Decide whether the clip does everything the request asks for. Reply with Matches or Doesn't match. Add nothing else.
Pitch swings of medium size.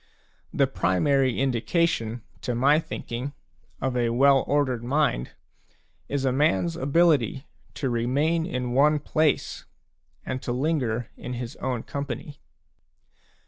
Matches